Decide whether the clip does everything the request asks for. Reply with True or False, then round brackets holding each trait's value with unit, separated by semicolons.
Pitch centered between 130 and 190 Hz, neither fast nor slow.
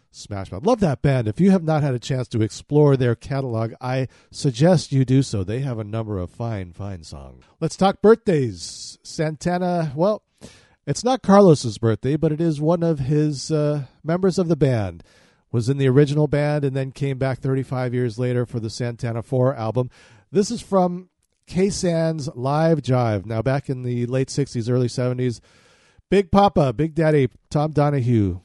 True (135 Hz; 185 wpm)